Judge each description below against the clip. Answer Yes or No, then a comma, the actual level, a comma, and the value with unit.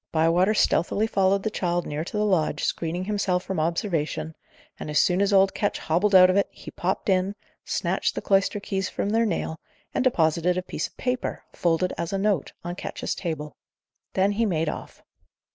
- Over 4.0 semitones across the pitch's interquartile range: No, average, 3.3 semitones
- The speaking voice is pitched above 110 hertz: Yes, medium, 185 Hz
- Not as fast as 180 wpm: No, average, 195 wpm